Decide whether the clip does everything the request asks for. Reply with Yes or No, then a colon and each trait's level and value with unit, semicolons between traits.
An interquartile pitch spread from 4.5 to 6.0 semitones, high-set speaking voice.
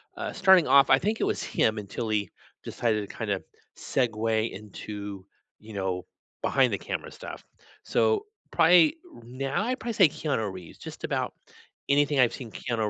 No: wide, 5.6 semitones; low, 120 Hz